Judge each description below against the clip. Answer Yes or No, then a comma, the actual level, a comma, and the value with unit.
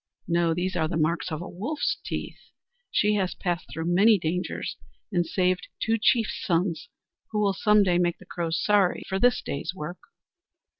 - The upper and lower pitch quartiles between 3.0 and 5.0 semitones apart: Yes, average, 3.3 semitones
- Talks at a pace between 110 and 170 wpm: No, average, 180 wpm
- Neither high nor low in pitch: Yes, medium, 180 Hz